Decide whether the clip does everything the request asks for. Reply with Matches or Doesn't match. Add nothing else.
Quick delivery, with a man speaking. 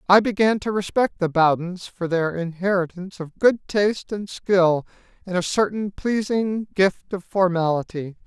Doesn't match